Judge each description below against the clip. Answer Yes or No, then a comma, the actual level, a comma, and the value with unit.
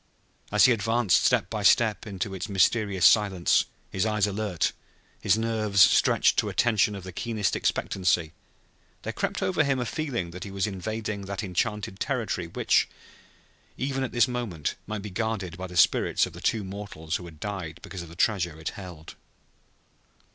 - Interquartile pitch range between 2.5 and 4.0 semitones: Yes, average, 3.4 semitones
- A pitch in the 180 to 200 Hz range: No, low, 100 Hz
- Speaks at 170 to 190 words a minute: Yes, average, 175 wpm